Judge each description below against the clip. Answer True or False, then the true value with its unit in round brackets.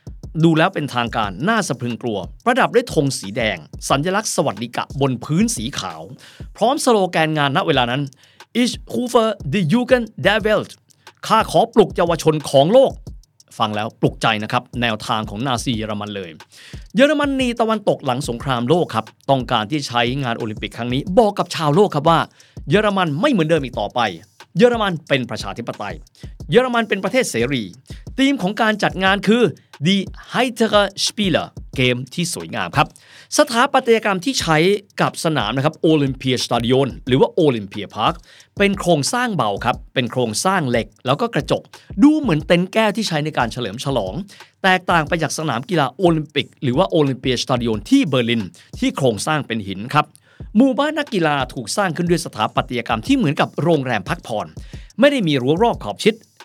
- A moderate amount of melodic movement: False (8.5 semitones)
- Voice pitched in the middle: True (155 Hz)